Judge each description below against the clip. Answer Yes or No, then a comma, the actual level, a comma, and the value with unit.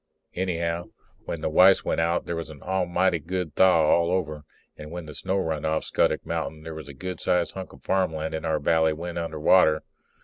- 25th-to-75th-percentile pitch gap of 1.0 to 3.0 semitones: Yes, narrow, 2.5 semitones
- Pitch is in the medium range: No, very low, 85 Hz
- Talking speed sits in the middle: No, fast, 210 wpm